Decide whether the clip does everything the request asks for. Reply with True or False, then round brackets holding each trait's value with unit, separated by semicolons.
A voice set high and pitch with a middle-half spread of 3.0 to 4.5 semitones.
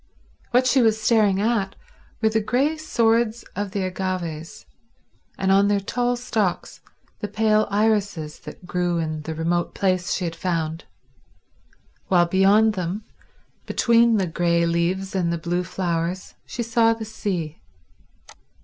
True (195 Hz; 4.2 semitones)